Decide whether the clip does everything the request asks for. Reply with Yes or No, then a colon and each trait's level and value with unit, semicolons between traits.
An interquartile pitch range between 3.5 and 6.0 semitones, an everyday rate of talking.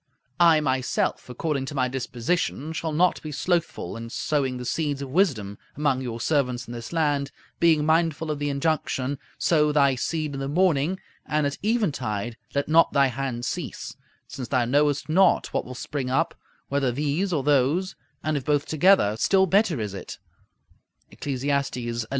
Yes: average, 3.8 semitones; average, 175 wpm